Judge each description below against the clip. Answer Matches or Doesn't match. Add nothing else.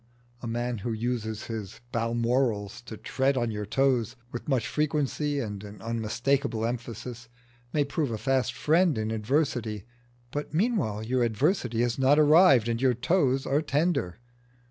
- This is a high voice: Doesn't match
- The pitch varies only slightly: Doesn't match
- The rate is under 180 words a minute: Matches